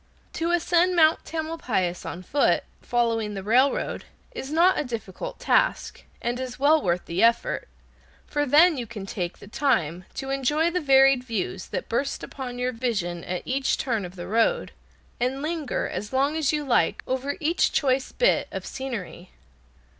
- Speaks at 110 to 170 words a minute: Yes, average, 165 wpm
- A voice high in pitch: Yes, very high, 260 Hz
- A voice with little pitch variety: No, wide, 5.4 semitones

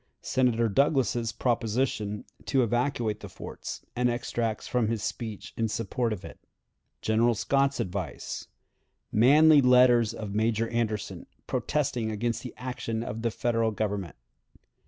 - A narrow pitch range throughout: Yes, narrow, 2.3 semitones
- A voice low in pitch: Yes, low, 115 Hz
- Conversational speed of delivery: No, slow, 130 wpm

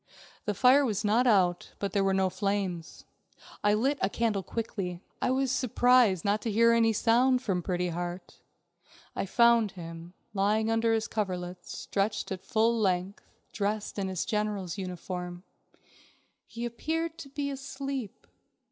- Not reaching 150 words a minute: No, average, 155 wpm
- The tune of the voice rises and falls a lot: No, average, 3.9 semitones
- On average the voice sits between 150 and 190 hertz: No, high, 210 Hz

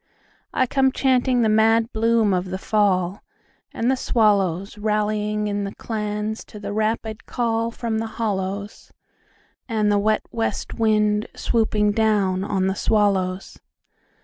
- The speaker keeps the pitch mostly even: Yes, narrow, 1.9 semitones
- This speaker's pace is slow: Yes, slow, 120 wpm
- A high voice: Yes, high, 215 Hz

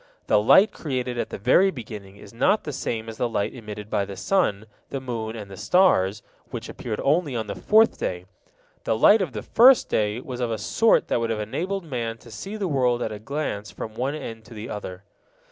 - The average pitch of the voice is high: No, low, 115 Hz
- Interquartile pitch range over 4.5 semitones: Yes, wide, 5.6 semitones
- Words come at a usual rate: No, fast, 225 wpm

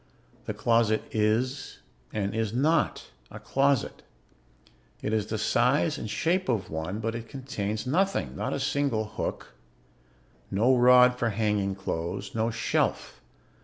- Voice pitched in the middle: No, low, 115 Hz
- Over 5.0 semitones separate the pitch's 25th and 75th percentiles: No, average, 3.8 semitones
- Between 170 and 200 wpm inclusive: No, slow, 135 wpm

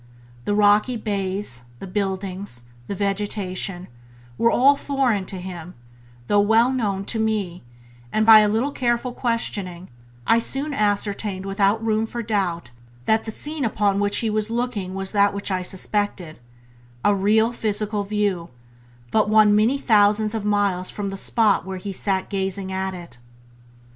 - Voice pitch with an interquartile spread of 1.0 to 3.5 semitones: Yes, narrow, 2.4 semitones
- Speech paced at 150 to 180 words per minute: Yes, average, 160 wpm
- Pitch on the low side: No, high, 205 Hz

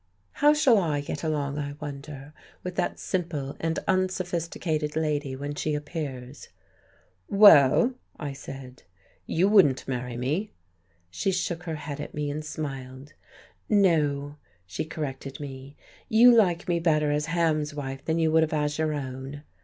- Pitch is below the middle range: No, medium, 150 Hz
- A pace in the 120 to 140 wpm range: No, average, 150 wpm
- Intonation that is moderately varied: Yes, average, 3.1 semitones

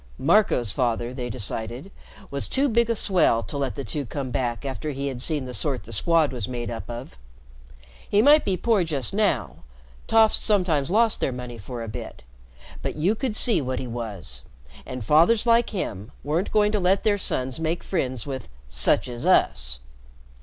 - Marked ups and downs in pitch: Yes, wide, 8.3 semitones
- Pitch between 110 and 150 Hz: Yes, medium, 140 Hz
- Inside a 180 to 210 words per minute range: Yes, average, 190 wpm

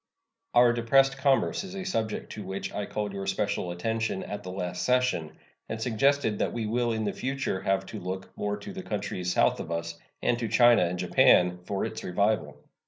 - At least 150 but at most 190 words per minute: No, average, 200 wpm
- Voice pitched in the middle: No, low, 105 Hz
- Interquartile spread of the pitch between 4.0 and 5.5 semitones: Yes, average, 4.3 semitones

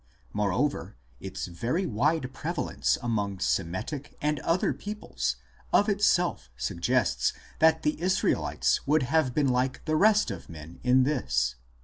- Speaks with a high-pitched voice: No, low, 135 Hz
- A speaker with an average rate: No, slow, 130 wpm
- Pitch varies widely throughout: Yes, wide, 7.6 semitones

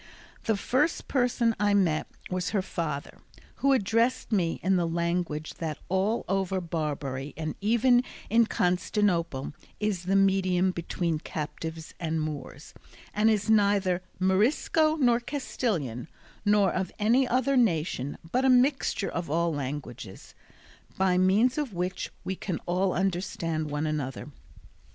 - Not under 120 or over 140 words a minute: Yes, slow, 135 wpm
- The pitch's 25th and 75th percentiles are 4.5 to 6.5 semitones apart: Yes, average, 5.1 semitones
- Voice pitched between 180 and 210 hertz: Yes, medium, 185 Hz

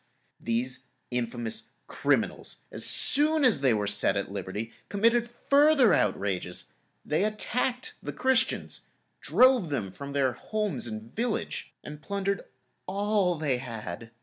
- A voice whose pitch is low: No, medium, 150 Hz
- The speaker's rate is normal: No, slow, 125 wpm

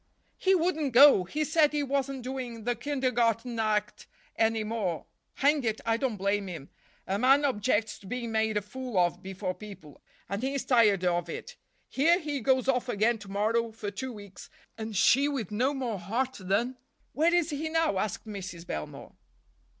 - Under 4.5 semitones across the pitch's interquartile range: No, average, 4.8 semitones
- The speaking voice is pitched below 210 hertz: No, high, 230 Hz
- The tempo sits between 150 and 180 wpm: Yes, average, 175 wpm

